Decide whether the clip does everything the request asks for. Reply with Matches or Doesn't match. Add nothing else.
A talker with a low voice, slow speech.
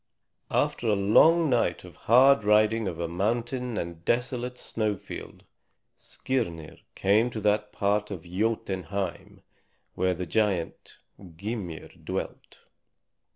Matches